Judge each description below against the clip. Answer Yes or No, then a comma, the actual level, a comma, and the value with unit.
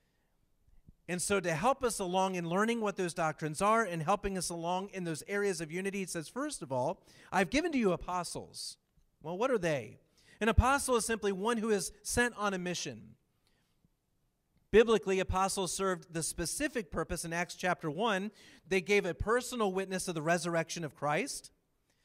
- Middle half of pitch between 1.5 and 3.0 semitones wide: No, average, 3.7 semitones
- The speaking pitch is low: No, high, 190 Hz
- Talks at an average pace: Yes, average, 180 wpm